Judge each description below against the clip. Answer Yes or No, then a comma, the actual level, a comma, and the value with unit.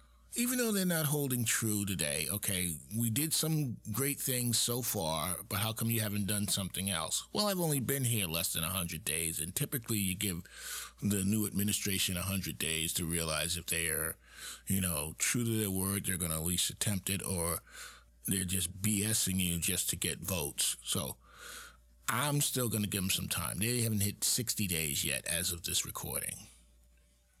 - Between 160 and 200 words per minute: Yes, average, 195 wpm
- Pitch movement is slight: No, average, 5.2 semitones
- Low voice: Yes, very low, 95 Hz